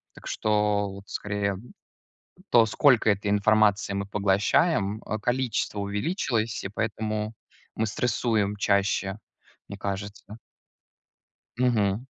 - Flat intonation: Yes, narrow, 1.7 semitones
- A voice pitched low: Yes, low, 105 Hz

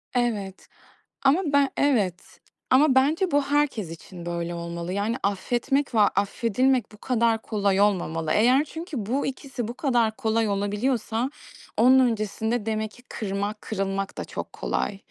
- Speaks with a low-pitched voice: No, high, 225 Hz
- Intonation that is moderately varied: Yes, average, 4.8 semitones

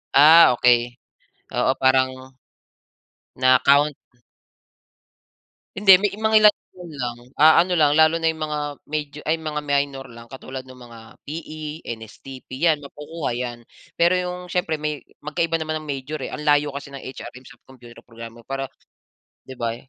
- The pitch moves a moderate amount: Yes, average, 3.5 semitones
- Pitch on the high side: No, medium, 145 Hz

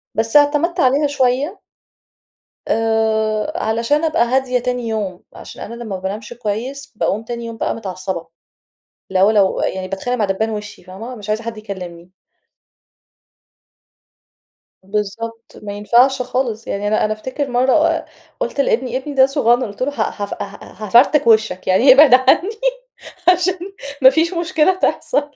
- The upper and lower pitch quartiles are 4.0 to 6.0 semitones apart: Yes, average, 4.3 semitones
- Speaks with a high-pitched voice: Yes, high, 230 Hz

